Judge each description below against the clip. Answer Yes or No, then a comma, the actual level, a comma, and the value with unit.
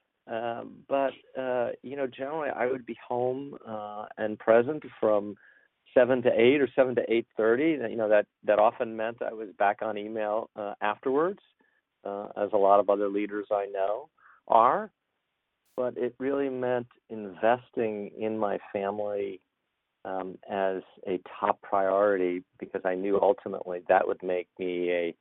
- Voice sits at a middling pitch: No, low, 105 Hz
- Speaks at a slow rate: No, average, 160 wpm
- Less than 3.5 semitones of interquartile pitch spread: Yes, average, 3.1 semitones